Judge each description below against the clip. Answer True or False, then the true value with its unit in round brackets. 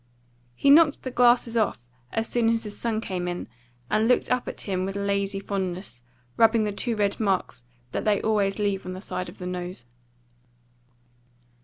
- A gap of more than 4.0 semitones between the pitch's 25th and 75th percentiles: False (3.4 semitones)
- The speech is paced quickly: False (170 wpm)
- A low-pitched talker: False (205 Hz)